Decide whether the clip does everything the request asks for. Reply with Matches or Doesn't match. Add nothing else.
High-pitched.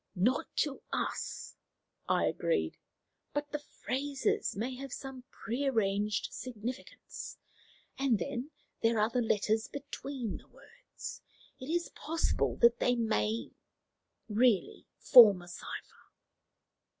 Matches